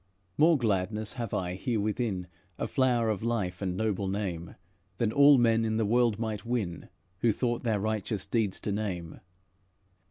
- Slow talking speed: No, average, 160 wpm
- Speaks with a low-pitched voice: Yes, low, 110 Hz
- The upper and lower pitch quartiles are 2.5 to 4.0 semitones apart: Yes, average, 3.3 semitones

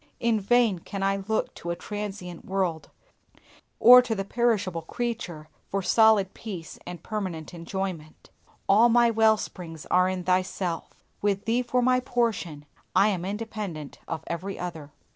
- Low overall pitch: No, high, 195 Hz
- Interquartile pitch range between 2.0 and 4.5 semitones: Yes, average, 4.2 semitones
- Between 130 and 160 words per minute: Yes, average, 150 wpm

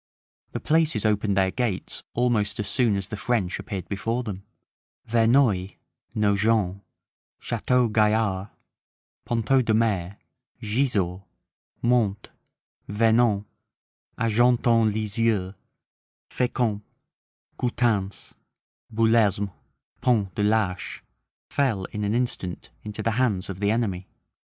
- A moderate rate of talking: No, slow, 100 wpm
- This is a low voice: Yes, low, 110 Hz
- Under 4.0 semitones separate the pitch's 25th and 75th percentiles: Yes, average, 2.9 semitones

